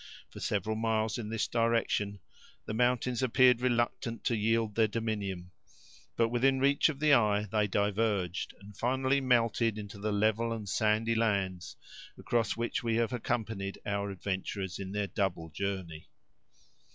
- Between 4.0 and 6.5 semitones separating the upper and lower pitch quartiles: No, narrow, 2.6 semitones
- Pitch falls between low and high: No, low, 110 Hz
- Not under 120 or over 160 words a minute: Yes, average, 150 wpm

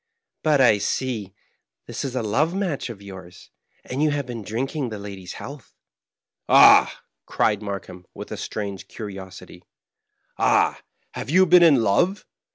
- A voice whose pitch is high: No, low, 115 Hz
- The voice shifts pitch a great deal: Yes, wide, 6.3 semitones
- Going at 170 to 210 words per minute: No, average, 160 wpm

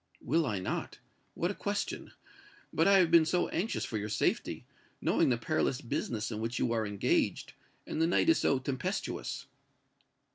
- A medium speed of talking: Yes, average, 175 wpm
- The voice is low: Yes, low, 130 Hz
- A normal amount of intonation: No, wide, 6.9 semitones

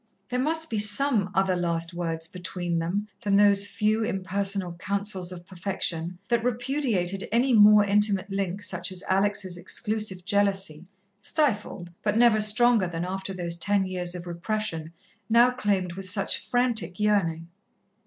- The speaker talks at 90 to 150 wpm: Yes, average, 145 wpm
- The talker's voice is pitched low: No, high, 195 Hz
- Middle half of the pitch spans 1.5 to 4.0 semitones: Yes, average, 3.1 semitones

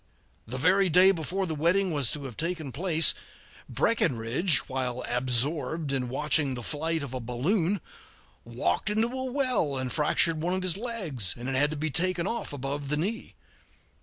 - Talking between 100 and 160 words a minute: No, average, 175 wpm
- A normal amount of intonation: No, wide, 5.7 semitones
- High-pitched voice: No, medium, 155 Hz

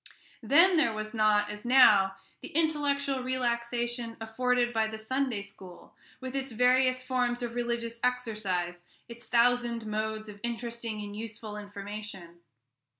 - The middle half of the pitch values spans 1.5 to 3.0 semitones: Yes, average, 2.7 semitones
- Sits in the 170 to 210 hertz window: No, high, 235 Hz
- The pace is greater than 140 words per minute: No, slow, 135 wpm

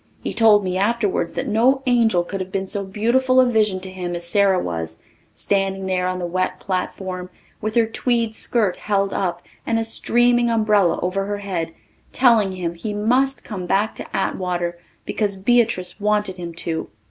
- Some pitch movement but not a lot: Yes, average, 3.6 semitones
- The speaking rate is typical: Yes, average, 180 wpm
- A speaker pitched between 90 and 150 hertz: No, high, 195 Hz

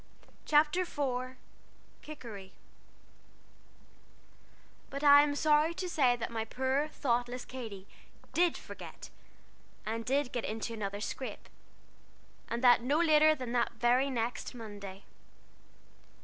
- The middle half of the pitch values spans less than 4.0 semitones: No, average, 4.3 semitones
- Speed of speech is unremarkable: No, slow, 120 wpm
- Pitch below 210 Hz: No, very high, 255 Hz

